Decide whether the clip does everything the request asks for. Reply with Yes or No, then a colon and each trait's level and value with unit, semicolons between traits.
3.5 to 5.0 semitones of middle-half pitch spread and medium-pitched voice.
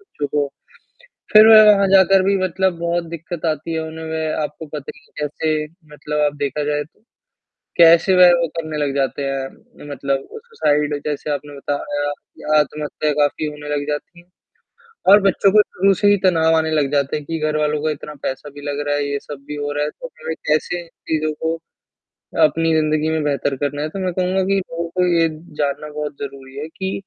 No: average, 2.7 semitones; medium, 155 Hz